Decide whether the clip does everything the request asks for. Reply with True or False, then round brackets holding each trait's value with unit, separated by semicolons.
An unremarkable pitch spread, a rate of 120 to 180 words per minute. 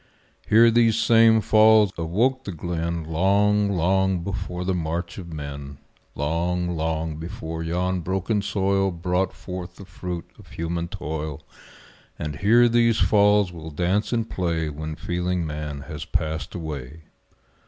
True (3.8 semitones; 140 wpm)